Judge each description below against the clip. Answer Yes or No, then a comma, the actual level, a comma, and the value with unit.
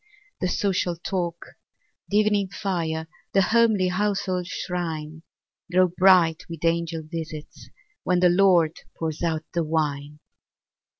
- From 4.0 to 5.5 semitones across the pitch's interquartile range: No, average, 2.8 semitones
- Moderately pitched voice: Yes, medium, 175 Hz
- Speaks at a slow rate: Yes, slow, 120 wpm